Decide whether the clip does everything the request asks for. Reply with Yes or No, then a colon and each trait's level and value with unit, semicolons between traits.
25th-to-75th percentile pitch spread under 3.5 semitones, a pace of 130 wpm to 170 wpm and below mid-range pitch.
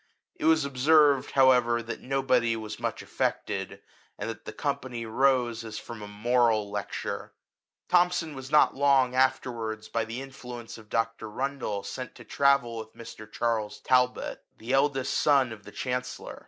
Yes: average, 3.1 semitones; average, 155 wpm; low, 125 Hz